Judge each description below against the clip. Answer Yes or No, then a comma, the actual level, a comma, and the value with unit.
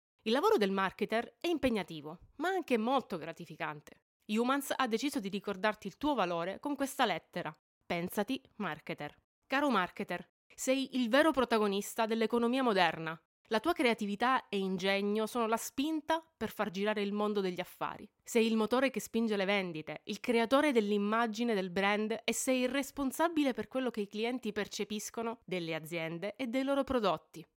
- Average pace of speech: Yes, average, 160 wpm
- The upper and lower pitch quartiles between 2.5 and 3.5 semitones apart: No, average, 4.6 semitones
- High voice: Yes, high, 225 Hz